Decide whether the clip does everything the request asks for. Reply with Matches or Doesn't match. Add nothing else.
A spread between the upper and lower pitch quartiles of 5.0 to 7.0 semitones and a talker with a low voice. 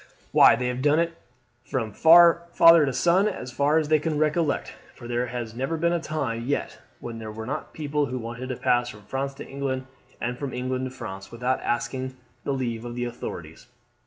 Doesn't match